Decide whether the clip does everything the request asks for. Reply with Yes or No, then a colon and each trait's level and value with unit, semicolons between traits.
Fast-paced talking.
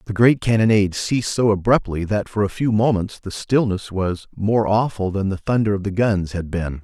Yes: fast, 210 wpm